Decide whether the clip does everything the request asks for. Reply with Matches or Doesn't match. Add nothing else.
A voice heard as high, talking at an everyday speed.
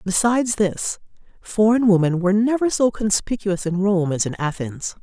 Matches